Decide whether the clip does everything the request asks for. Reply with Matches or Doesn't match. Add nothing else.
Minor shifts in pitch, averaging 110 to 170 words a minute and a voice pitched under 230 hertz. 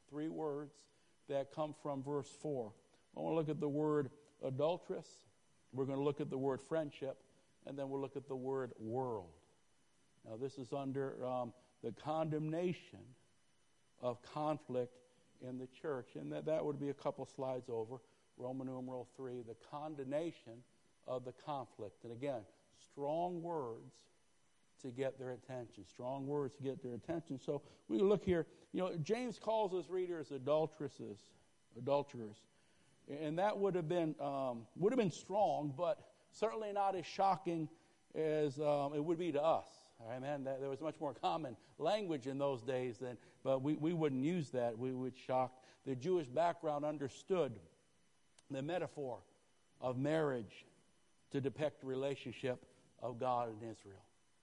Doesn't match